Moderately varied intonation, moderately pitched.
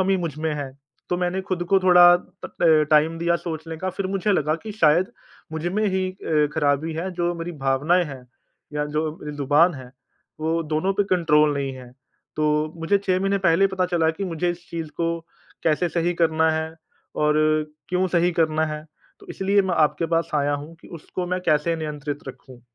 Yes: average, 3.0 semitones; medium, 165 Hz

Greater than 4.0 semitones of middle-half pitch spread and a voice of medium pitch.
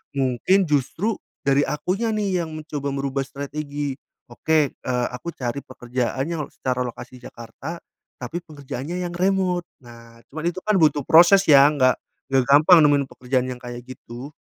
Yes: average, 4.8 semitones; medium, 145 Hz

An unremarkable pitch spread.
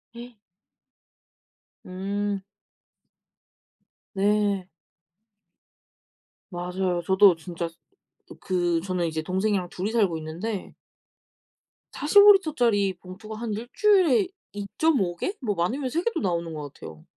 Yes: average, 4.9 semitones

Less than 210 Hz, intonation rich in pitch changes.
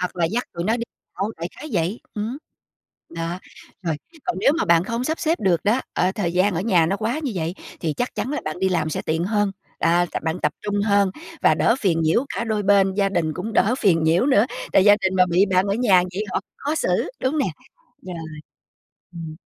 No: high, 195 Hz; average, 4.6 semitones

